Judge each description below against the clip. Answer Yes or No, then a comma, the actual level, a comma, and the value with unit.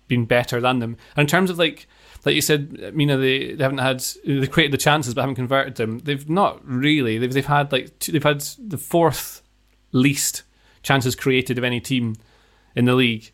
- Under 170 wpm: No, average, 200 wpm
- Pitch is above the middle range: No, low, 135 Hz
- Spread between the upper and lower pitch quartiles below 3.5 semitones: Yes, average, 2.8 semitones